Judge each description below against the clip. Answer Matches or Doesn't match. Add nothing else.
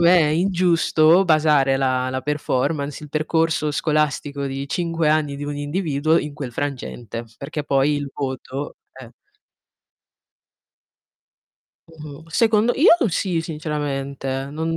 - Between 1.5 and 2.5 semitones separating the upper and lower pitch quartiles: Doesn't match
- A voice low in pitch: Doesn't match